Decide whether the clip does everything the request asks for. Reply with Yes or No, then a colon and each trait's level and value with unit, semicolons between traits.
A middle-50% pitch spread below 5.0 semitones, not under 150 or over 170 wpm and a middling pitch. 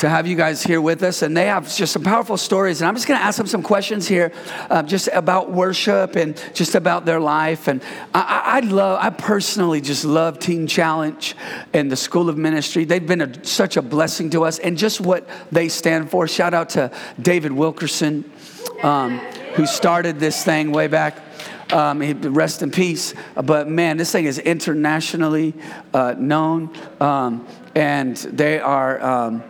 No: average, 2.9 semitones; average, 185 wpm; medium, 165 Hz